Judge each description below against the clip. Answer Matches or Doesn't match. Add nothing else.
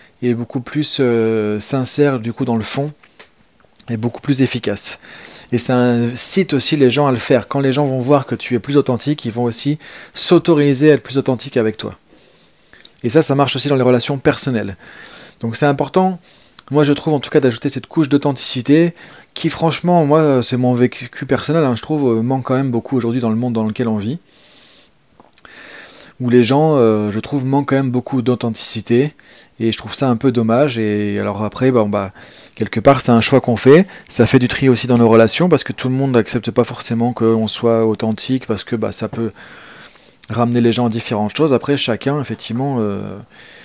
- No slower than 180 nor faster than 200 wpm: Doesn't match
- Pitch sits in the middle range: Doesn't match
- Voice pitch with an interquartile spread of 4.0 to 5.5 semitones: Doesn't match